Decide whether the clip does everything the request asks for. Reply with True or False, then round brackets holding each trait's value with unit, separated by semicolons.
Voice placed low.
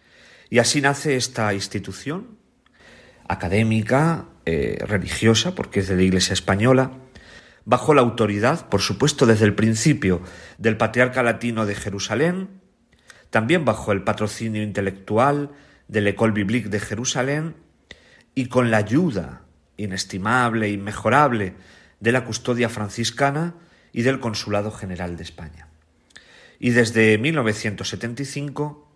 True (110 Hz)